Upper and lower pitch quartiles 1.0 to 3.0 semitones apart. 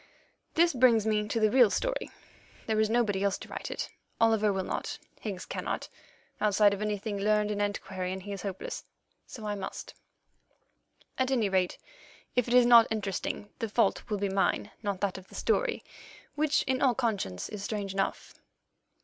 Yes: average, 2.7 semitones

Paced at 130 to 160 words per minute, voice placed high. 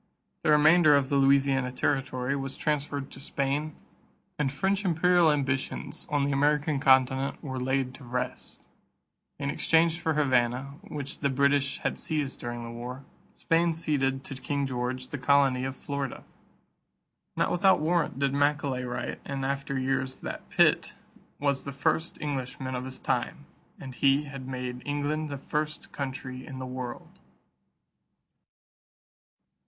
No: average, 145 wpm; medium, 140 Hz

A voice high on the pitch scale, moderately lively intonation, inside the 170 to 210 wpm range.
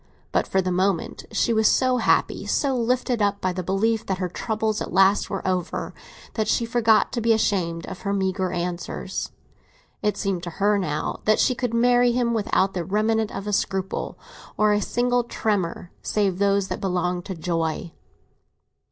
Yes: high, 200 Hz; average, 3.4 semitones; average, 180 wpm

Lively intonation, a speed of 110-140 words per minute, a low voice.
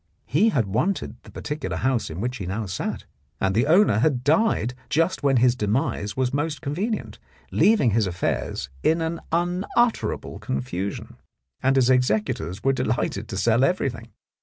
No: wide, 6.9 semitones; average, 155 wpm; low, 130 Hz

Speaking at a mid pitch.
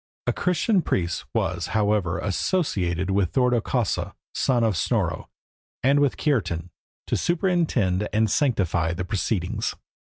No: low, 105 Hz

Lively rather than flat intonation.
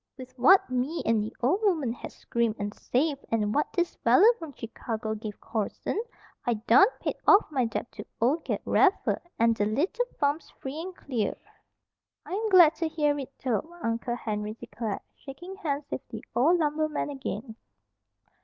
Yes: wide, 6.0 semitones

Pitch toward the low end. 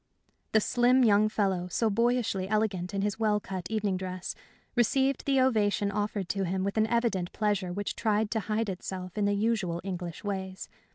No: high, 205 Hz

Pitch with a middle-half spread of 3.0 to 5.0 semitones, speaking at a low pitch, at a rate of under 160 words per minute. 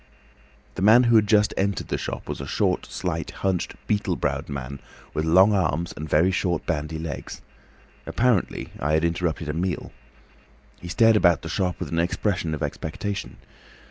No: average, 4.2 semitones; very low, 90 Hz; average, 175 wpm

